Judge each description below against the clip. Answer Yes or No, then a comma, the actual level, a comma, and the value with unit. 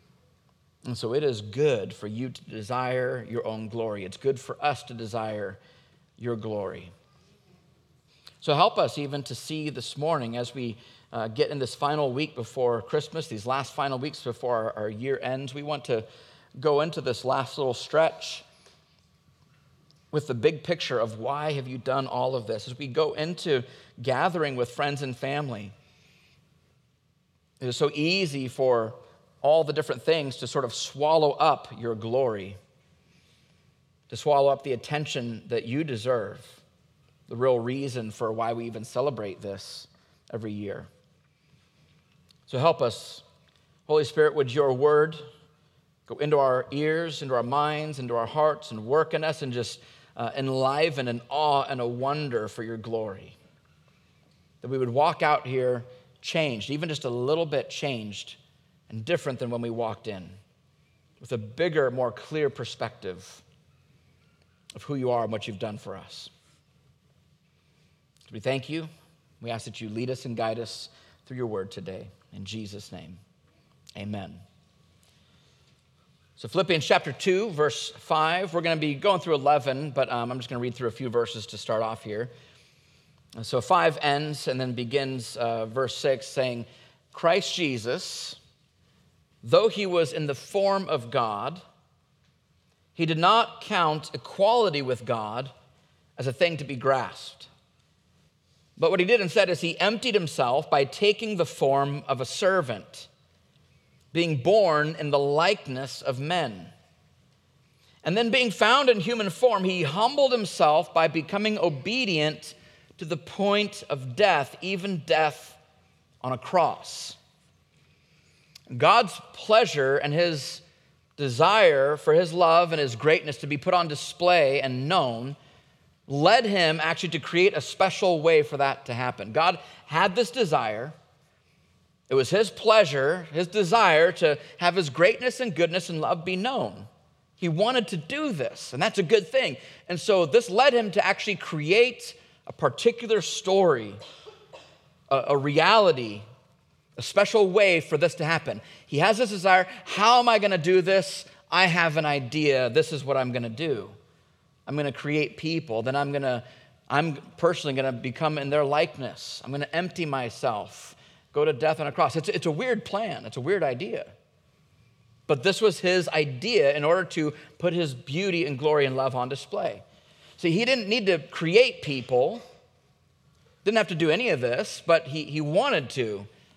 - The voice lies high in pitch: No, medium, 145 Hz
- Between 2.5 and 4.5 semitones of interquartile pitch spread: No, average, 5.1 semitones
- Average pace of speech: Yes, average, 165 wpm